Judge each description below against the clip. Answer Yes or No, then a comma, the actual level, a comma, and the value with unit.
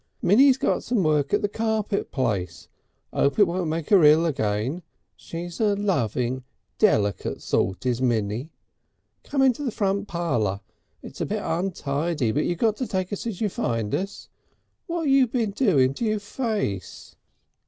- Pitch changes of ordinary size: No, wide, 8.6 semitones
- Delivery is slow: No, average, 165 wpm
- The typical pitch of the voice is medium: Yes, medium, 175 Hz